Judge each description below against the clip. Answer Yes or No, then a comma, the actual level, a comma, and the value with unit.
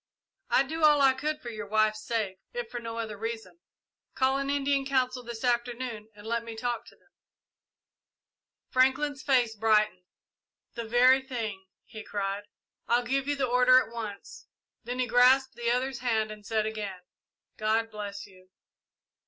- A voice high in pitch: Yes, high, 235 Hz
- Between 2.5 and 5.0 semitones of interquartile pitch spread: Yes, average, 3.2 semitones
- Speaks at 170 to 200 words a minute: No, average, 160 wpm